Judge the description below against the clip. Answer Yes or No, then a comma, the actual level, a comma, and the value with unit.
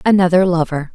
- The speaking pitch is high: No, medium, 175 Hz